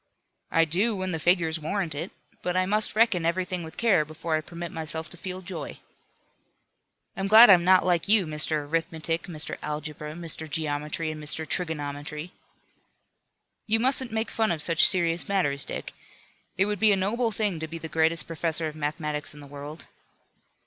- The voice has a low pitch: No, medium, 165 Hz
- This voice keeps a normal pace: Yes, average, 175 wpm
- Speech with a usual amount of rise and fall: Yes, average, 3.3 semitones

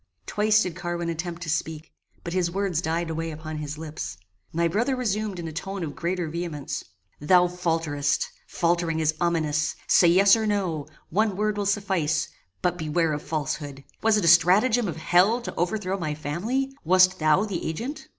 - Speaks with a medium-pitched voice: Yes, medium, 170 Hz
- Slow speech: No, average, 180 wpm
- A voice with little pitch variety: No, average, 3.7 semitones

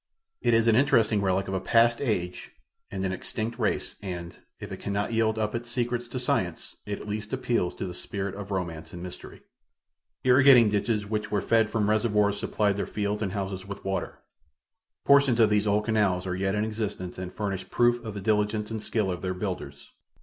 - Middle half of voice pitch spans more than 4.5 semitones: No, average, 2.9 semitones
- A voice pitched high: No, low, 105 Hz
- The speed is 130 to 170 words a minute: No, average, 200 wpm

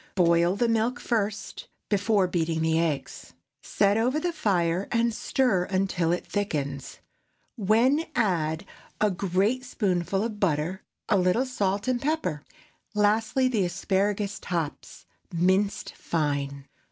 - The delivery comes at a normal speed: No, slow, 130 wpm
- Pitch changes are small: No, average, 4.6 semitones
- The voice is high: Yes, high, 195 Hz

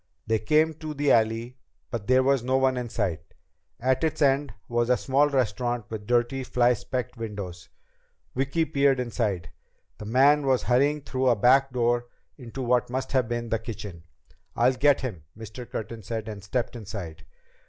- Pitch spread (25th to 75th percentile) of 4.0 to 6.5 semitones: No, average, 3.0 semitones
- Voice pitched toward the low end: Yes, low, 120 Hz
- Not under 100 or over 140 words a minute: No, average, 175 wpm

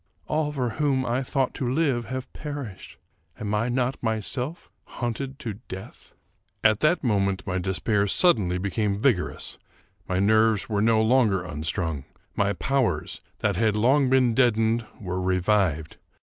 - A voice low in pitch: Yes, low, 110 Hz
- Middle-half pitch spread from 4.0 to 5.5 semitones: Yes, average, 4.8 semitones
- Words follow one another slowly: No, average, 150 wpm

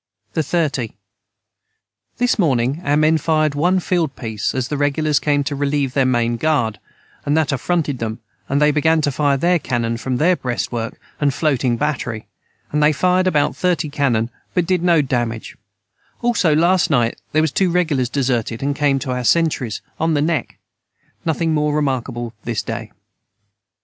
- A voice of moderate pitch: Yes, medium, 145 Hz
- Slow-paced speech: No, average, 170 wpm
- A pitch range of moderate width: Yes, average, 4.1 semitones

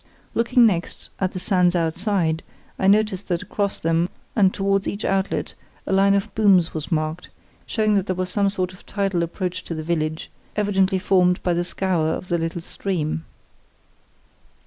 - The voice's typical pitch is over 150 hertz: Yes, medium, 185 Hz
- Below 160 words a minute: No, average, 170 wpm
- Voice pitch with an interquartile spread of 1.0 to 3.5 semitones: Yes, average, 2.7 semitones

